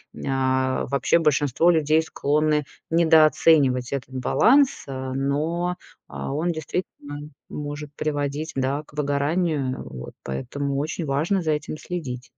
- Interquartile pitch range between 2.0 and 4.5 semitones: Yes, average, 2.8 semitones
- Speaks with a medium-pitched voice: Yes, medium, 145 Hz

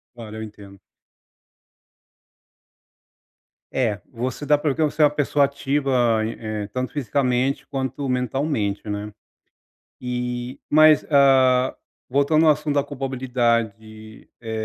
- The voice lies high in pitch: No, low, 130 Hz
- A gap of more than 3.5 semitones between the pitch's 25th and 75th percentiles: Yes, average, 4.1 semitones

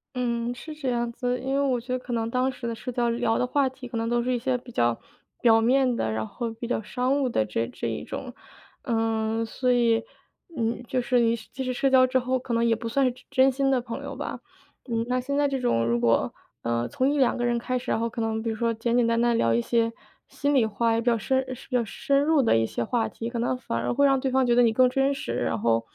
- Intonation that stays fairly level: Yes, narrow, 2.2 semitones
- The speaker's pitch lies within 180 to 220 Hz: No, high, 240 Hz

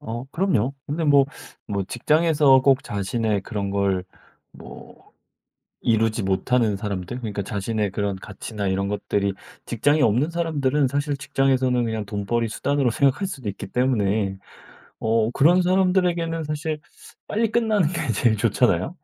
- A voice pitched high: No, low, 120 Hz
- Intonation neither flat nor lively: No, wide, 6.3 semitones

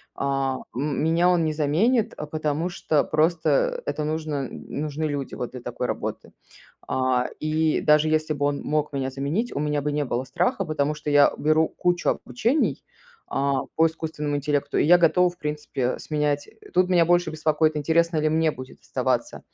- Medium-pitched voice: Yes, medium, 155 Hz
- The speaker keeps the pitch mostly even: Yes, narrow, 2.1 semitones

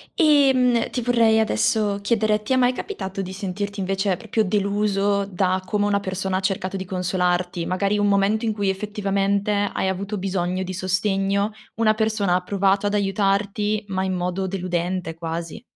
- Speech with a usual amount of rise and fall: No, narrow, 2.0 semitones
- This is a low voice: No, high, 195 Hz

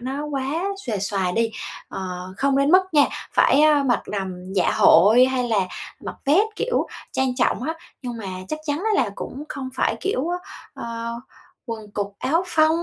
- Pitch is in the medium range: No, very high, 260 Hz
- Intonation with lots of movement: Yes, wide, 5.7 semitones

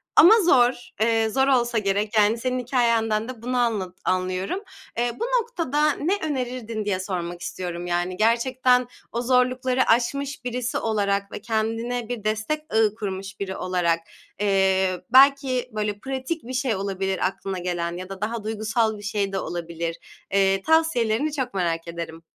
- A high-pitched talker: Yes, high, 220 Hz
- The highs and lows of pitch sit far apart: No, average, 4.6 semitones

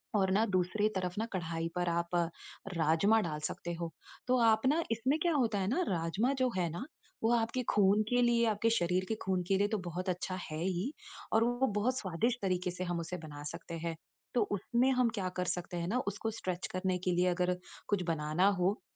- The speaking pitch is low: No, medium, 185 Hz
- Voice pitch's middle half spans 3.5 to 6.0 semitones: Yes, average, 4.3 semitones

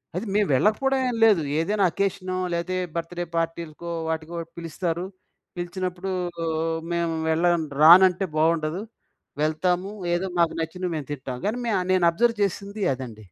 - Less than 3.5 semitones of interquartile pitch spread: Yes, average, 2.9 semitones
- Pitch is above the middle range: No, medium, 175 Hz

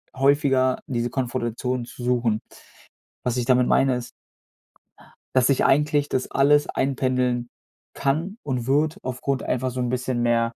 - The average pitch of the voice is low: Yes, low, 130 Hz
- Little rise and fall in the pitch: Yes, narrow, 2.0 semitones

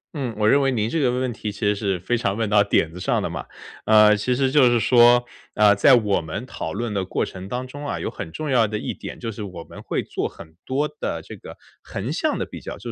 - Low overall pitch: Yes, low, 110 Hz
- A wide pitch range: No, average, 4.1 semitones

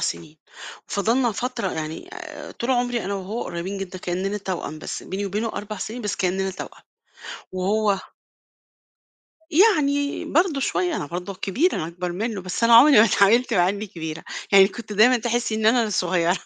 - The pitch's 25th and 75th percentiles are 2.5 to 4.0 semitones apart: No, average, 4.4 semitones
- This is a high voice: Yes, high, 205 Hz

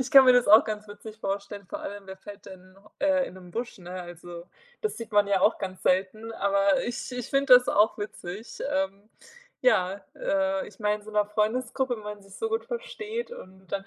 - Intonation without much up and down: No, average, 4.2 semitones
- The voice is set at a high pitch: Yes, high, 210 Hz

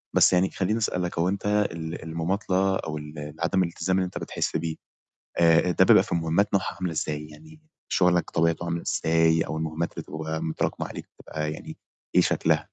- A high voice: No, very low, 85 Hz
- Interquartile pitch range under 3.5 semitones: Yes, average, 2.7 semitones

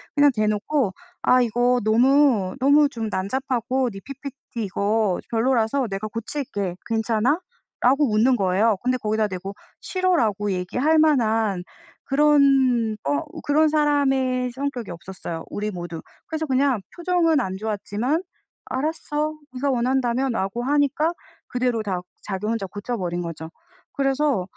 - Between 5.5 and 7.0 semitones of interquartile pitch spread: No, average, 5.1 semitones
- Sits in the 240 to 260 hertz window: Yes, high, 245 Hz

